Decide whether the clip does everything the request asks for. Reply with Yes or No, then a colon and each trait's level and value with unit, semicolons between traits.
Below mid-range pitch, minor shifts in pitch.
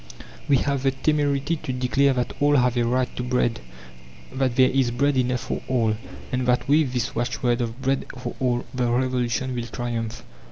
Yes: low, 125 Hz; narrow, 1.8 semitones